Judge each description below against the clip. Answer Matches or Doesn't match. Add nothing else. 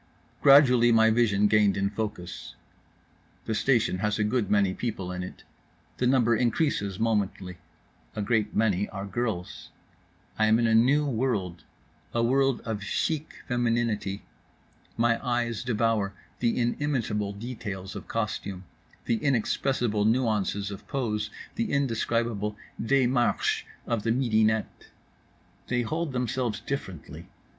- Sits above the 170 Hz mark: Doesn't match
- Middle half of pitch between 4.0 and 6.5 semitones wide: Doesn't match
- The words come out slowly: Matches